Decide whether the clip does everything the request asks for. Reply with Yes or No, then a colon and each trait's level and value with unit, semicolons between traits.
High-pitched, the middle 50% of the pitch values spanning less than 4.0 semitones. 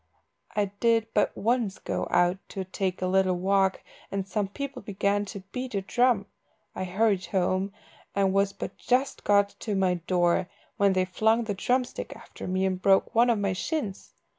Yes: high, 195 Hz; average, 2.8 semitones